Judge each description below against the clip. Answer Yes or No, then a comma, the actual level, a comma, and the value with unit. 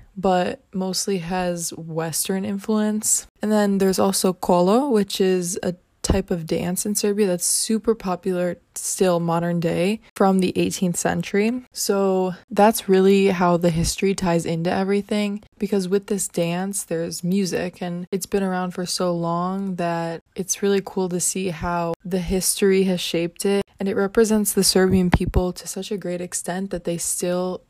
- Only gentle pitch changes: Yes, narrow, 2.1 semitones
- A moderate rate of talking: Yes, average, 165 wpm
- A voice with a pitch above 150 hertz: Yes, medium, 185 Hz